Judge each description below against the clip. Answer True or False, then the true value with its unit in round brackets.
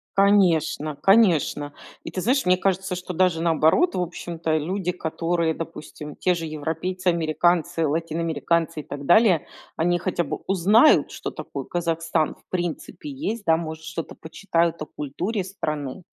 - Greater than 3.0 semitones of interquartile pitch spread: False (2.5 semitones)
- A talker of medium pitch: True (170 Hz)